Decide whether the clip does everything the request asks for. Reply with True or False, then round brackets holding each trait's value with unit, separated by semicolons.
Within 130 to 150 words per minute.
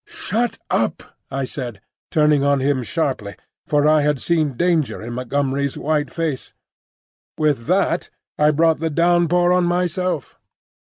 True (140 wpm)